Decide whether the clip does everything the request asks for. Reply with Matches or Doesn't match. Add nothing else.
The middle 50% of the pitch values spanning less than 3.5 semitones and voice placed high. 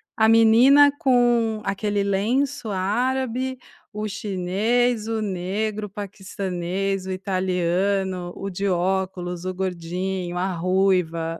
Matches